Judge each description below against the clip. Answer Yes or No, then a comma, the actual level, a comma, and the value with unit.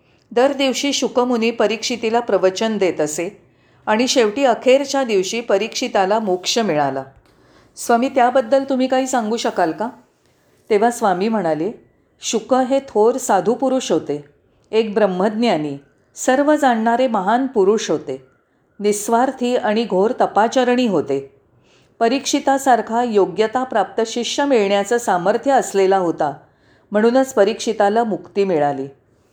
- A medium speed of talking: Yes, average, 110 wpm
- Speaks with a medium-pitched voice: No, high, 225 Hz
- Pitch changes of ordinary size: Yes, average, 4.7 semitones